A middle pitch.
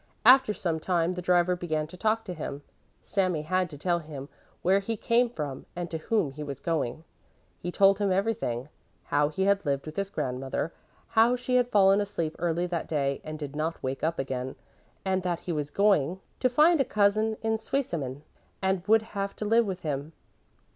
Yes: medium, 180 Hz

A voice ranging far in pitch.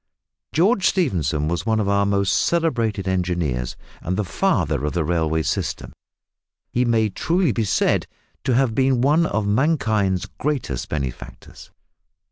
Yes: wide, 7.2 semitones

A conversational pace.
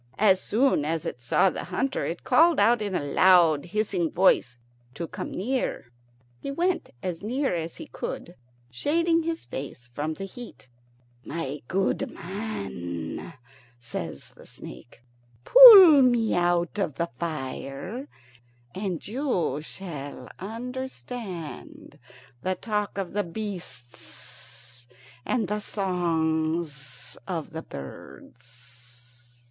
No: slow, 120 wpm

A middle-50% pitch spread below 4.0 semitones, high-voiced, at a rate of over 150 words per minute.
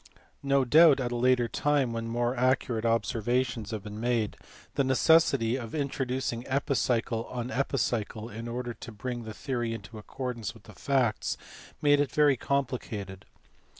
No: average, 2.7 semitones; low, 120 Hz; average, 160 wpm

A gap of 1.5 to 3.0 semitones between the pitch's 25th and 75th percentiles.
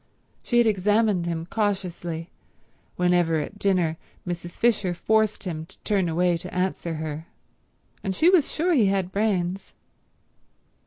No: average, 3.5 semitones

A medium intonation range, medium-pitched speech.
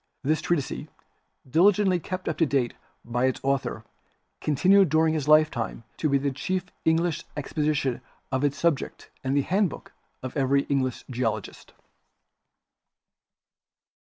Yes: average, 4.1 semitones; medium, 145 Hz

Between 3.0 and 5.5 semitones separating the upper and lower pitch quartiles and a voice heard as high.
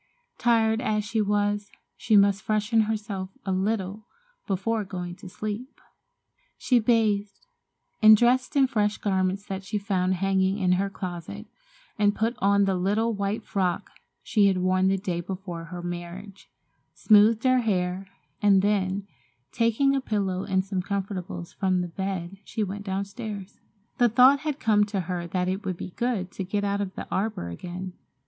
No: narrow, 2.4 semitones; high, 200 Hz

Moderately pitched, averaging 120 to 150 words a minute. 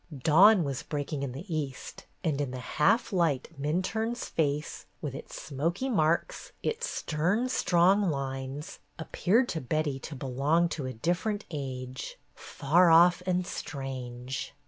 Yes: medium, 155 Hz; average, 140 wpm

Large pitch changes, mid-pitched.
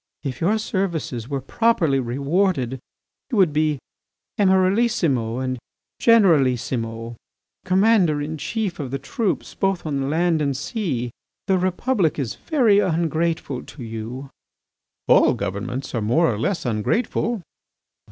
Yes: wide, 6.9 semitones; medium, 155 Hz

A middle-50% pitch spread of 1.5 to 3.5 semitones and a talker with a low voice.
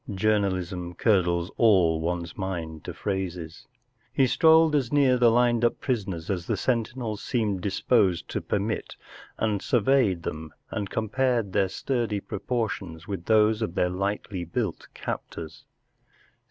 No: average, 4.8 semitones; low, 100 Hz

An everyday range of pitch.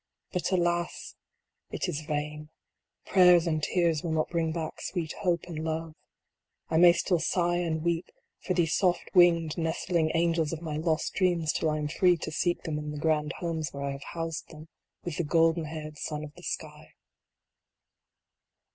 No: narrow, 2.0 semitones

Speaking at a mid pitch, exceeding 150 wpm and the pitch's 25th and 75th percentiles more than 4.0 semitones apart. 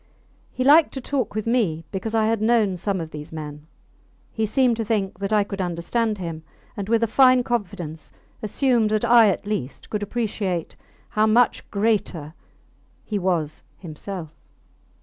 No: high, 210 Hz; average, 165 wpm; average, 4.5 semitones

